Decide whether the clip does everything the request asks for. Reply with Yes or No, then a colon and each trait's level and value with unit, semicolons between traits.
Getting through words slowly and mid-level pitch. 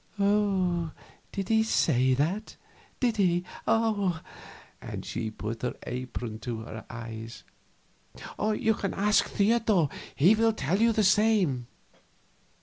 Yes: slow, 115 wpm; medium, 180 Hz